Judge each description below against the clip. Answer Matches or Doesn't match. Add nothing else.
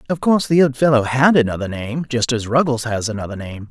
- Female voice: Doesn't match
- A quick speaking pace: Matches